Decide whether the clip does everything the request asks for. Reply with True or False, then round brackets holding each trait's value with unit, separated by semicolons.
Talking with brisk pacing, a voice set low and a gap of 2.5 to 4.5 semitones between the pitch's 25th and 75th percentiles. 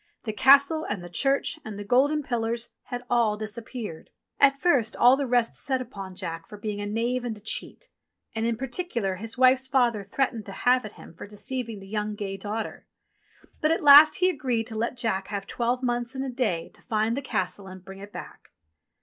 False (210 wpm; 230 Hz; 4.0 semitones)